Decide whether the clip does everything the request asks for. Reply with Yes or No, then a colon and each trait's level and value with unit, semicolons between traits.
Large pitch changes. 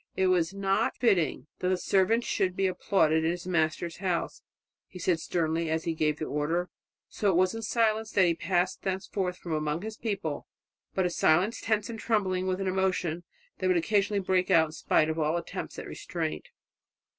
No: average, 2.9 semitones